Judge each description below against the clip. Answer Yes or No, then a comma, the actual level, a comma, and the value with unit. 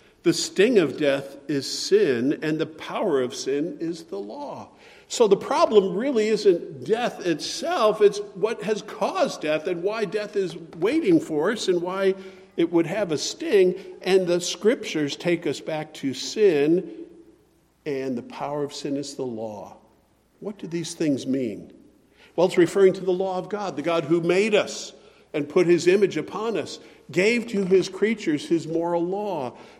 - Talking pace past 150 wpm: Yes, average, 175 wpm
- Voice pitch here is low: No, high, 190 Hz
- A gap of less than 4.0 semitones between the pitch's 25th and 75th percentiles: No, average, 4.8 semitones